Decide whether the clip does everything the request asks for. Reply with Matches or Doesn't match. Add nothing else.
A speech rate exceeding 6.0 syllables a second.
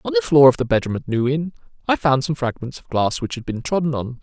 Matches